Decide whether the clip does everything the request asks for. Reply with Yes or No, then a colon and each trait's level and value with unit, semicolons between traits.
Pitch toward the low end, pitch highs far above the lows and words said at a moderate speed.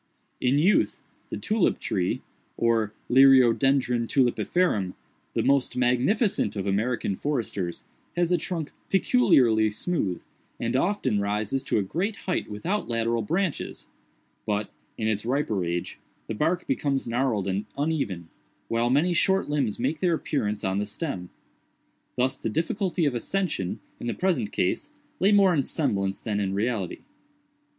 Yes: low, 125 Hz; wide, 7.7 semitones; average, 145 wpm